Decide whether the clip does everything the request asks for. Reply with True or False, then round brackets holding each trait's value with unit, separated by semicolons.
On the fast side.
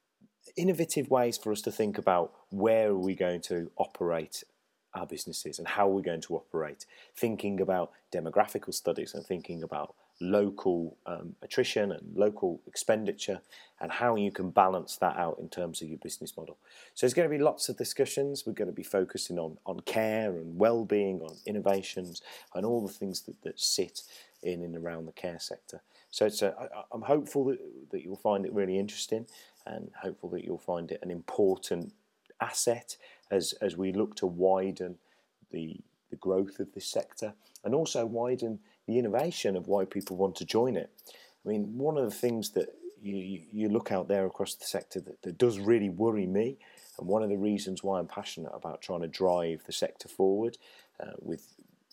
False (190 wpm)